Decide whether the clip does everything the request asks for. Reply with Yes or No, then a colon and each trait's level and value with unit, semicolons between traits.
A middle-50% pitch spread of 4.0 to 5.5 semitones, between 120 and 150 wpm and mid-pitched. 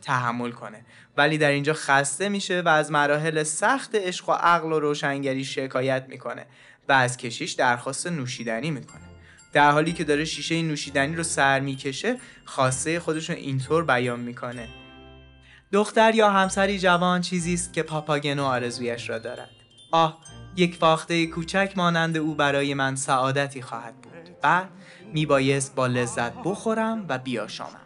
Yes: average, 4.5 semitones; average, 145 wpm; medium, 145 Hz